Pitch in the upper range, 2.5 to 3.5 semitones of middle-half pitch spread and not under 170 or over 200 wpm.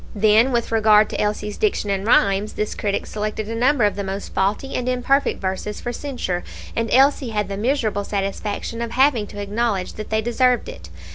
Yes: high, 215 Hz; average, 3.0 semitones; average, 195 wpm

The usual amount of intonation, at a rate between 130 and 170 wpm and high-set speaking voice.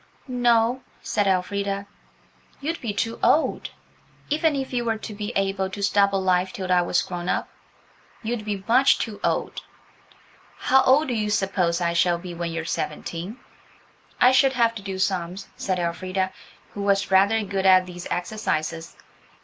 Yes: average, 3.6 semitones; average, 160 wpm; high, 195 Hz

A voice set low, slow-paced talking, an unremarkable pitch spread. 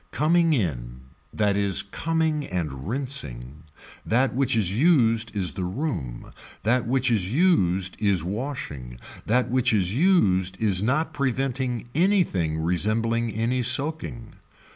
No: low, 115 Hz; slow, 125 wpm; wide, 6.6 semitones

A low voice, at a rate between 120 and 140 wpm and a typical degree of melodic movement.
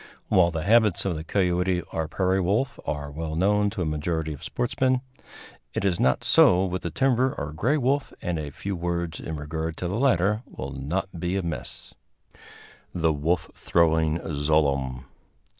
No: very low, 85 Hz; average, 175 wpm; average, 3.9 semitones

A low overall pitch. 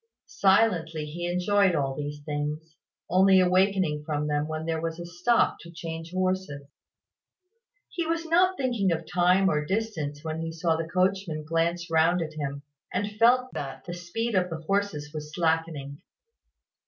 No: medium, 170 Hz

